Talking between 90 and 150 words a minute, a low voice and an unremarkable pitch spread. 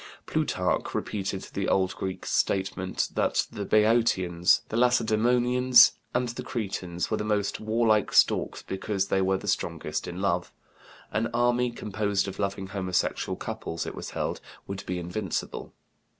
Yes: average, 145 wpm; low, 100 Hz; average, 3.2 semitones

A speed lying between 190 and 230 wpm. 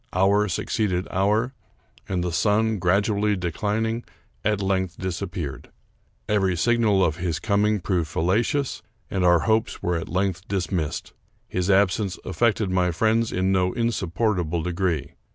No: average, 140 wpm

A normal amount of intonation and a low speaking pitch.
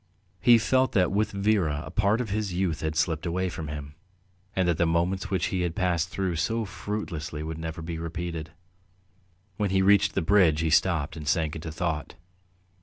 Yes: average, 3.4 semitones; very low, 85 Hz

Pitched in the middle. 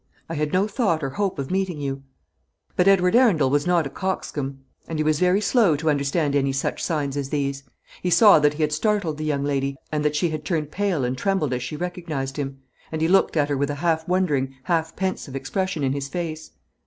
Yes: medium, 155 Hz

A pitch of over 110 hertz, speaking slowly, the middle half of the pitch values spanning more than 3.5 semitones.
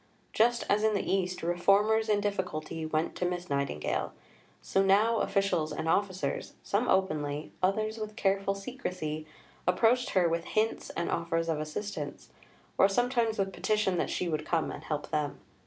No: high, 190 Hz; average, 160 wpm; average, 4.3 semitones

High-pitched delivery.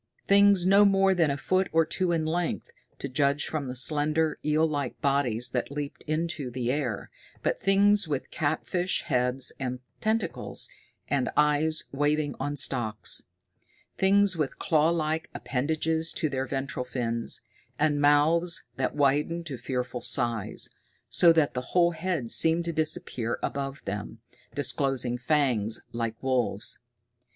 No: medium, 145 Hz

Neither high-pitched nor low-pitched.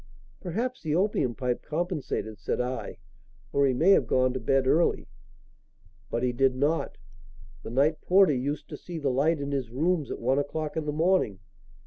Yes: medium, 145 Hz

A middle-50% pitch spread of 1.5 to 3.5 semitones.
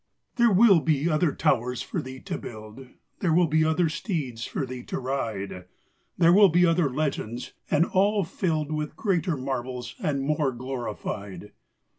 No: average, 5.3 semitones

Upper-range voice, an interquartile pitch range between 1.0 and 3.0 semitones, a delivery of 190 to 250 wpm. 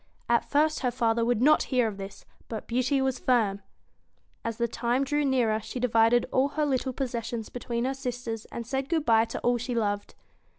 Yes: high, 245 Hz; narrow, 2.6 semitones; average, 200 wpm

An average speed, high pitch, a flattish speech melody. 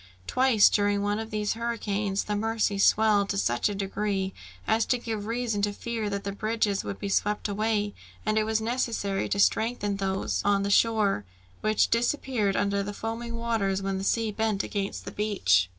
Yes: average, 185 wpm; high, 210 Hz; narrow, 1.9 semitones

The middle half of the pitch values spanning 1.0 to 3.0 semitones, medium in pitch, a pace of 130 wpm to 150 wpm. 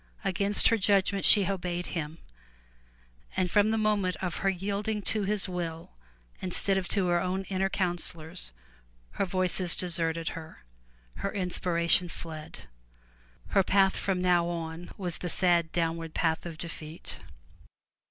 Yes: narrow, 2.4 semitones; medium, 180 Hz; average, 140 wpm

